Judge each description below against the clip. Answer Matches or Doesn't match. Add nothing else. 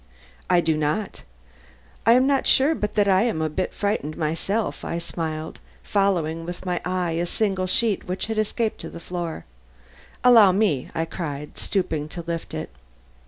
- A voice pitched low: Doesn't match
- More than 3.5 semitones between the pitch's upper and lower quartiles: Matches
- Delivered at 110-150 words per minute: Doesn't match